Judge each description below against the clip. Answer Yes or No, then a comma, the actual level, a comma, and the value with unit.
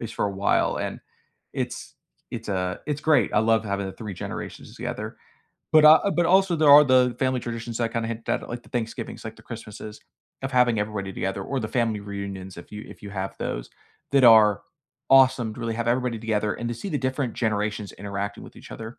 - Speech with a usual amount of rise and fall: Yes, average, 3.6 semitones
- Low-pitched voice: Yes, low, 115 Hz